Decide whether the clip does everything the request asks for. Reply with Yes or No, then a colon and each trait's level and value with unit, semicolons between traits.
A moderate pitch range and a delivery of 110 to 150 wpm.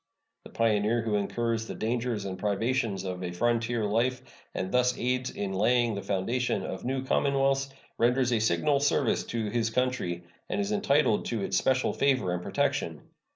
No: average, 3.8 semitones; average, 170 wpm